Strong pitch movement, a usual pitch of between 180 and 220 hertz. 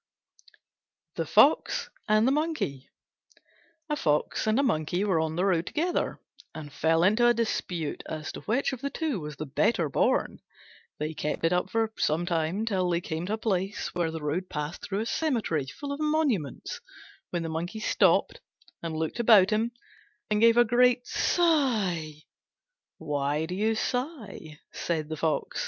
Yes: wide, 6.7 semitones; medium, 185 Hz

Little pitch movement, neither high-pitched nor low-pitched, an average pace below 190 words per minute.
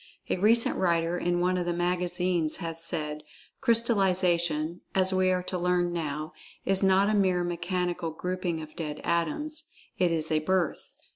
Yes: narrow, 2.0 semitones; medium, 175 Hz; average, 160 wpm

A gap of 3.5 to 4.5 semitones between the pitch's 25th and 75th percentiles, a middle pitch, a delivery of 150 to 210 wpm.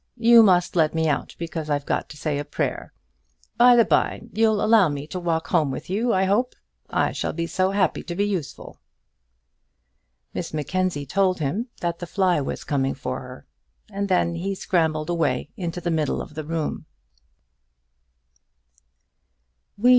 Yes: average, 4.2 semitones; medium, 170 Hz; average, 165 wpm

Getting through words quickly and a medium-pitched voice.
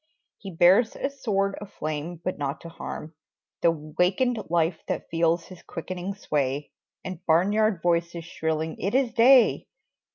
No: average, 150 wpm; medium, 175 Hz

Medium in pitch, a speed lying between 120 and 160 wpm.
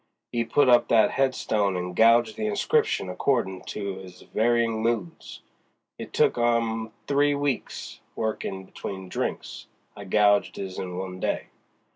No: low, 110 Hz; average, 140 wpm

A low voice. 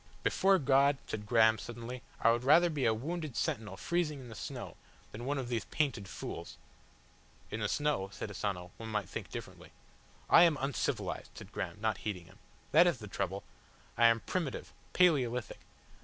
Yes: low, 120 Hz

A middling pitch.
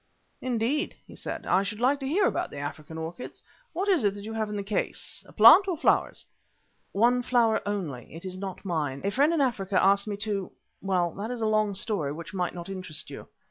No: high, 205 Hz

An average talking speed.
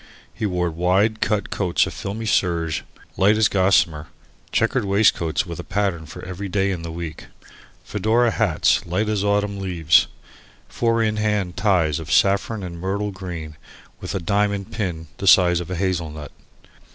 Yes: average, 165 wpm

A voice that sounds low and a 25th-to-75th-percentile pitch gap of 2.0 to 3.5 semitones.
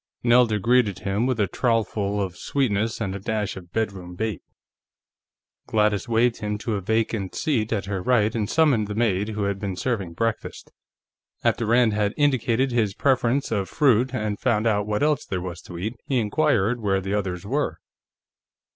Yes: low, 110 Hz; average, 3.2 semitones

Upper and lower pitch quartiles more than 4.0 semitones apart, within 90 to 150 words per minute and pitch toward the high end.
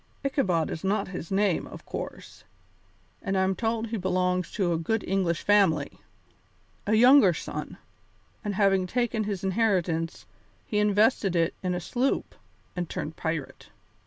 No: average, 3.4 semitones; average, 145 wpm; high, 195 Hz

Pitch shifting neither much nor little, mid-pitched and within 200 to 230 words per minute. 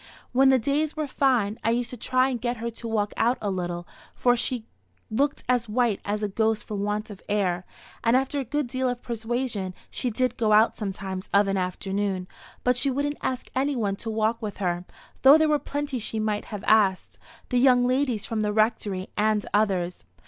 No: average, 3.7 semitones; high, 225 Hz; fast, 205 wpm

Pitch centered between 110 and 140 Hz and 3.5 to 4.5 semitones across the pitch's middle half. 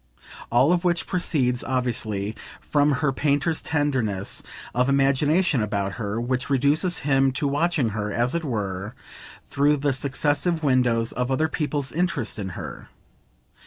Yes: low, 135 Hz; average, 4.0 semitones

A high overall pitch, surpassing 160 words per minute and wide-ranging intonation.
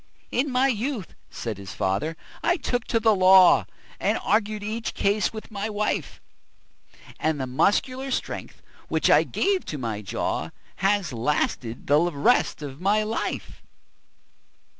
No: high, 205 Hz; average, 140 wpm; wide, 7.8 semitones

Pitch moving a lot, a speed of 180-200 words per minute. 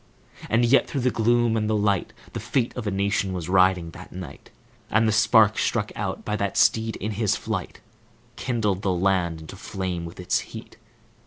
No: average, 3.2 semitones; average, 190 wpm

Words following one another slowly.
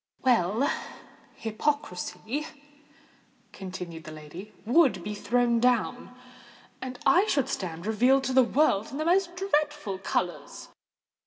Yes: slow, 105 wpm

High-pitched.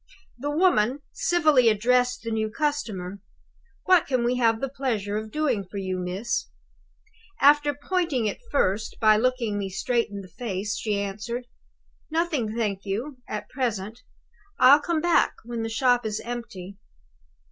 Yes: high, 235 Hz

